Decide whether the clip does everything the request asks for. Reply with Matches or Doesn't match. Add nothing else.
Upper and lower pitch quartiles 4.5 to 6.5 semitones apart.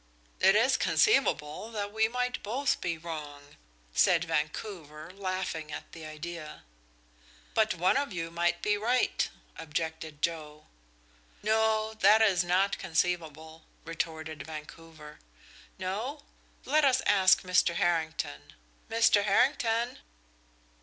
Matches